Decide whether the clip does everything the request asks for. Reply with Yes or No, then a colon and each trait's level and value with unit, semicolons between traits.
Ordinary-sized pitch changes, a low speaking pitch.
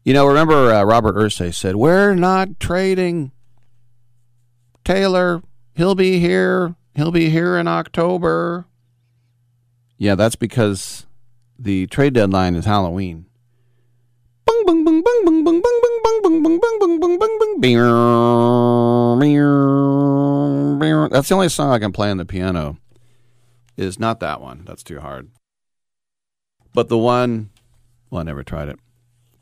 No: wide, 6.4 semitones; low, 120 Hz